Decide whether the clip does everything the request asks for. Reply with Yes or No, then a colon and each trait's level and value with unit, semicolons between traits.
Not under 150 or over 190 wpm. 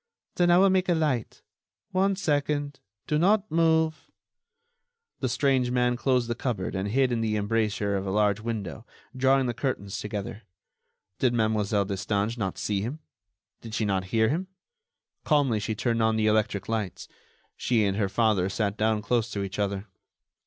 Yes: average, 170 wpm